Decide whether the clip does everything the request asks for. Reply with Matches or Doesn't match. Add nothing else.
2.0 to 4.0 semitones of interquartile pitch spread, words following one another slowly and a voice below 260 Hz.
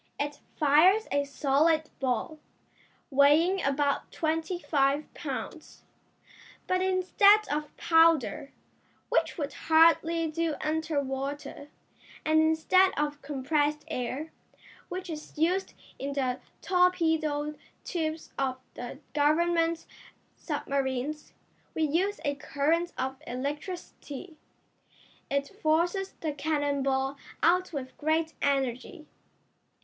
Doesn't match